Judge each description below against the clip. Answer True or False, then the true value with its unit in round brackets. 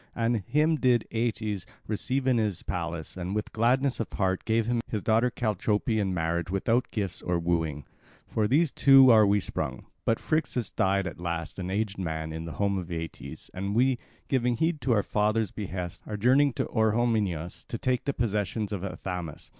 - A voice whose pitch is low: True (105 Hz)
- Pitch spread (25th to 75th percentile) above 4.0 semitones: True (4.8 semitones)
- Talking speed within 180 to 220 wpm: True (185 wpm)